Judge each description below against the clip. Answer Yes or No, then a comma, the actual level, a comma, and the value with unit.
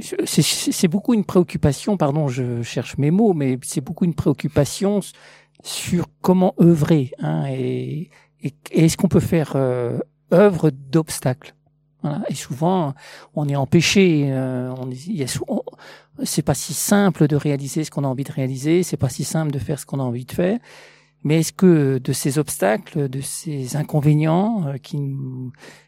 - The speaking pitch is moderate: Yes, medium, 150 Hz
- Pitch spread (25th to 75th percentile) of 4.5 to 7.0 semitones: No, average, 4.1 semitones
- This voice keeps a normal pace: Yes, average, 180 wpm